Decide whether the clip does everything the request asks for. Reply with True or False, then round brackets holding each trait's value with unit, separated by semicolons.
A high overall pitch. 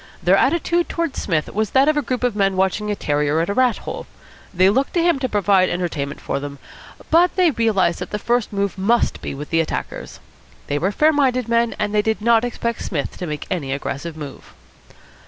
True (210 Hz)